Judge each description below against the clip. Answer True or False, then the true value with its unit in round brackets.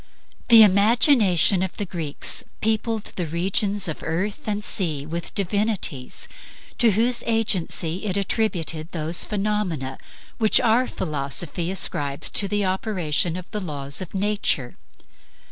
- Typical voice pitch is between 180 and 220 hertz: True (190 Hz)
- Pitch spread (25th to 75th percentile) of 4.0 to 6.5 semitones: True (4.4 semitones)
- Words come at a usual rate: False (130 wpm)